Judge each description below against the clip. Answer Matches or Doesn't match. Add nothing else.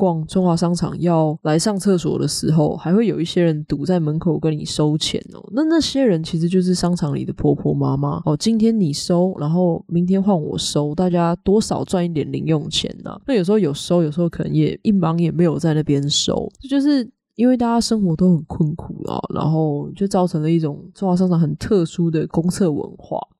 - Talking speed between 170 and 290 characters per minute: Doesn't match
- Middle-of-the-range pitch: Matches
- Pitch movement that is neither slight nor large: Matches